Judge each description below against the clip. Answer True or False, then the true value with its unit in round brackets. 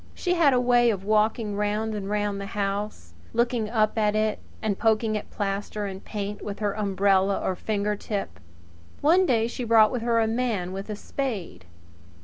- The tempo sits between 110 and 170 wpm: False (185 wpm)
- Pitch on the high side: True (210 Hz)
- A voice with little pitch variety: True (2.2 semitones)